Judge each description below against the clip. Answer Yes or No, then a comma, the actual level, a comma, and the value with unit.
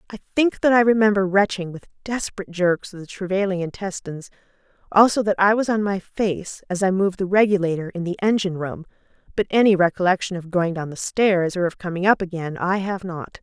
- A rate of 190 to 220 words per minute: Yes, average, 200 wpm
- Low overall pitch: No, high, 190 Hz